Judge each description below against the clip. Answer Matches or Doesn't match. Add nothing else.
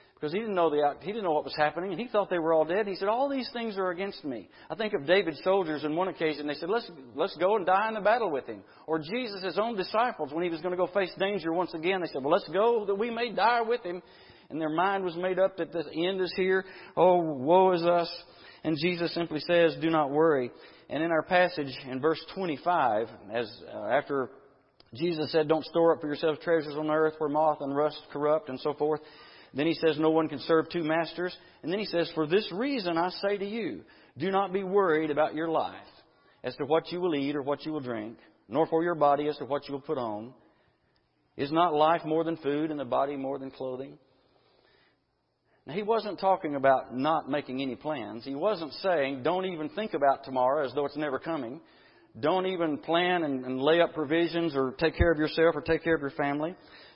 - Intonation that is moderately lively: Matches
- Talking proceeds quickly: Matches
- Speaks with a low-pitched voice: Doesn't match